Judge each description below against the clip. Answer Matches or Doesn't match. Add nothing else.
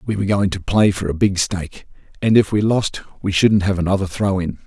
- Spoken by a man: Matches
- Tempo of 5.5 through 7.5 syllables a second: Matches